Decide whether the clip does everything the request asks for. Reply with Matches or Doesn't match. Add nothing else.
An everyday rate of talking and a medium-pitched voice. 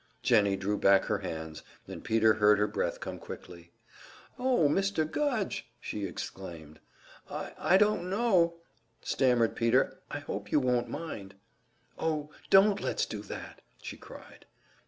Doesn't match